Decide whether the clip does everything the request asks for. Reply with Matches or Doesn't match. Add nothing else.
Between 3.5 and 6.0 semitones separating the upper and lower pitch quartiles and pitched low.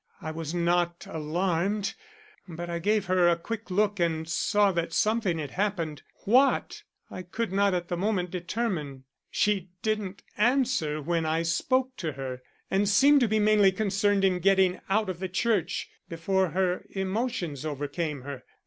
Doesn't match